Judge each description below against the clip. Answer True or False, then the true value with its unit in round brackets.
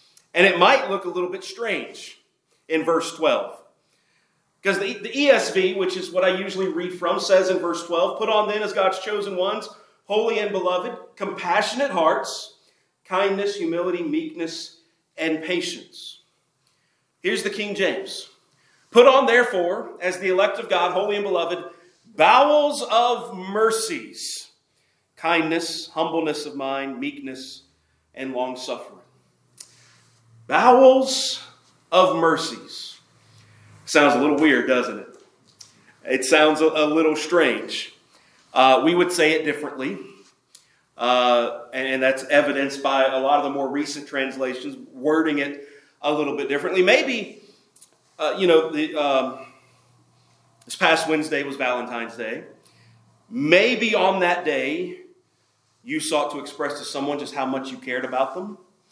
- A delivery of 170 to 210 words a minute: False (140 wpm)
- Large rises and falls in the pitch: True (5.8 semitones)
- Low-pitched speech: False (165 Hz)